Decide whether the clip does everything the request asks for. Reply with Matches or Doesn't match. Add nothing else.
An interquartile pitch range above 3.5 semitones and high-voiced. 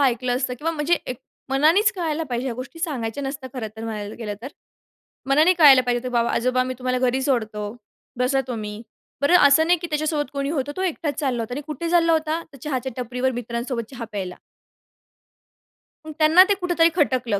Matches